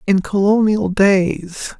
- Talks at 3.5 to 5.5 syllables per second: No, 3.1 syllables/s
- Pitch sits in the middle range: No, high, 195 Hz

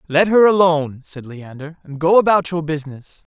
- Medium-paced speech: Yes, average, 180 wpm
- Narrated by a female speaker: No, male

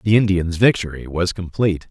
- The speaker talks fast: No, average, 155 wpm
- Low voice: Yes, very low, 95 Hz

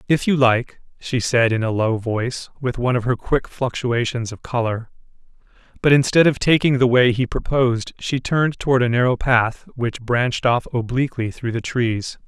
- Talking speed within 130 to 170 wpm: No, average, 185 wpm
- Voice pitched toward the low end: Yes, low, 125 Hz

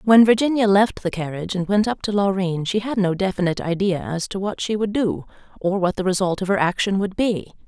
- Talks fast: Yes, fast, 235 wpm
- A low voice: No, high, 195 Hz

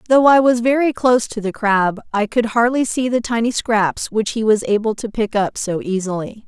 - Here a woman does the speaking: Yes, female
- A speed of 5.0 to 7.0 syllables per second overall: Yes, 5.1 syllables/s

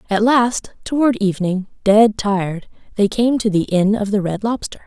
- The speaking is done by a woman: Yes, female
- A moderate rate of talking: Yes, average, 185 wpm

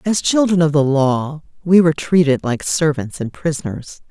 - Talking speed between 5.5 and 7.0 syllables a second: No, 4.8 syllables/s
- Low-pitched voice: No, medium, 155 Hz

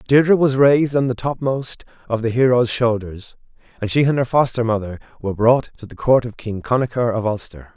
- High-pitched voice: No, low, 120 Hz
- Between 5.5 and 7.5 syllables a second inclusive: Yes, 5.6 syllables/s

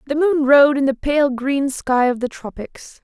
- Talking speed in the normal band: No, fast, 220 wpm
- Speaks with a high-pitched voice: Yes, very high, 275 Hz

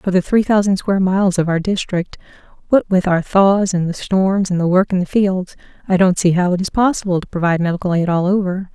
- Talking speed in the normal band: No, fast, 240 wpm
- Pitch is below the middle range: No, medium, 185 Hz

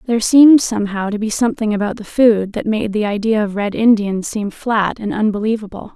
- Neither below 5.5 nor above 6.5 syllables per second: Yes, 5.7 syllables/s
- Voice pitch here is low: No, high, 215 Hz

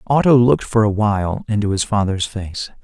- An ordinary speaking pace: Yes, average, 190 wpm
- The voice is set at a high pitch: No, low, 105 Hz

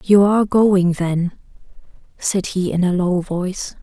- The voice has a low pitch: No, medium, 185 Hz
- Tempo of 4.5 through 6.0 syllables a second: No, 4.2 syllables/s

